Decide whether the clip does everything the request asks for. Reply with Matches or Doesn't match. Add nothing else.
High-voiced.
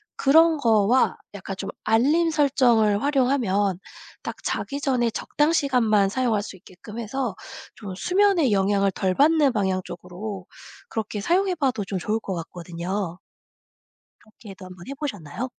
Matches